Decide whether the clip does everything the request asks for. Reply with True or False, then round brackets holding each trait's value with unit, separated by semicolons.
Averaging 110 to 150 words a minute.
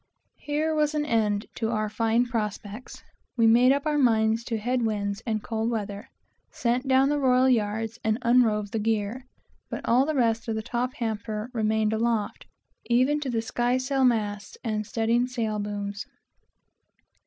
False (165 wpm)